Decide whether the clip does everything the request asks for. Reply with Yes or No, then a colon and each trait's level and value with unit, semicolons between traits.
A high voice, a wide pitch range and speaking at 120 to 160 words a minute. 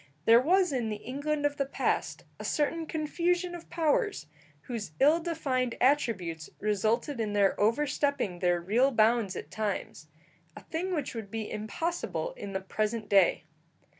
Yes: very high, 250 Hz; wide, 6.4 semitones; average, 155 wpm